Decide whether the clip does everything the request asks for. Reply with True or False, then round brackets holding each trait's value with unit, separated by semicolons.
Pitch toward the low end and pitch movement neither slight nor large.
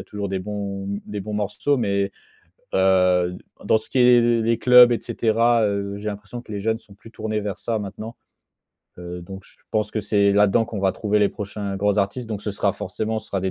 False (105 Hz; 2.0 semitones)